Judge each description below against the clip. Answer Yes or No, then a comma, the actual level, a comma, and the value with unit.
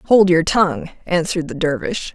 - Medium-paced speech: Yes, average, 170 wpm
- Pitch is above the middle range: No, medium, 170 Hz